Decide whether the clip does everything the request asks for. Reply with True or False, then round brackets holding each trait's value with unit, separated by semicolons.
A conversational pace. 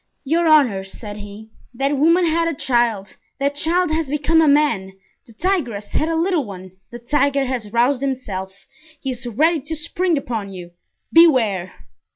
True (165 wpm)